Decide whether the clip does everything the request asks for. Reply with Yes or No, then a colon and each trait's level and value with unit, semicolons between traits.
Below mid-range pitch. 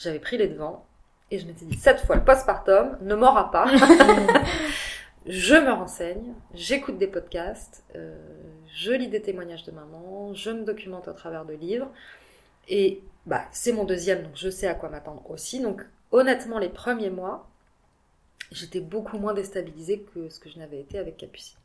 No: high, 190 Hz